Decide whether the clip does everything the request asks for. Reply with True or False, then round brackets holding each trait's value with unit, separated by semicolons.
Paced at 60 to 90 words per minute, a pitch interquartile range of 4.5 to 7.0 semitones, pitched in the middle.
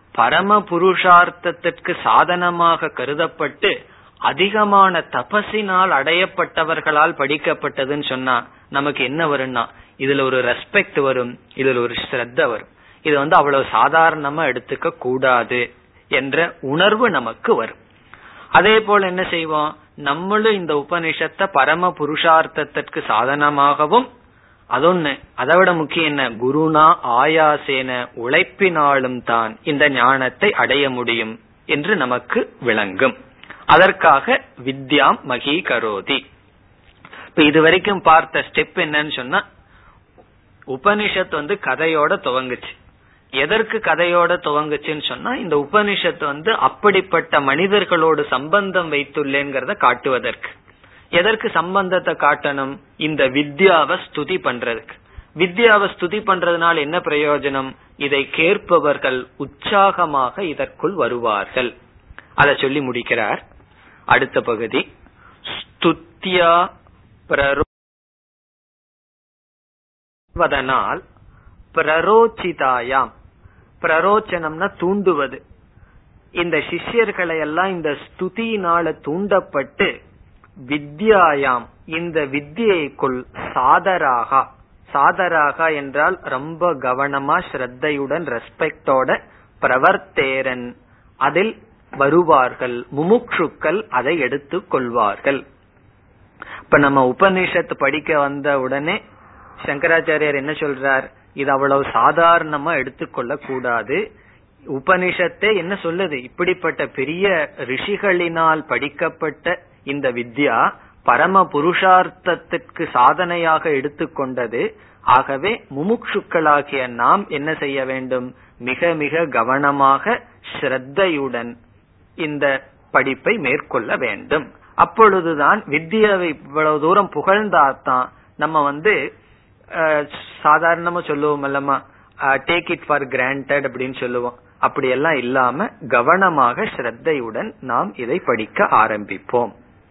True (80 wpm; 4.8 semitones; 150 Hz)